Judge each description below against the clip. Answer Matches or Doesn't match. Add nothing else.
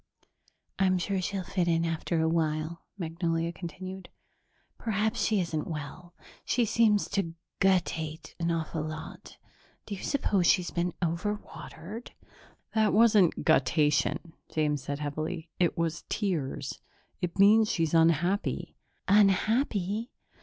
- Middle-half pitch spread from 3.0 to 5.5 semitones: Matches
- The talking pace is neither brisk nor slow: Doesn't match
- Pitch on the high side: Doesn't match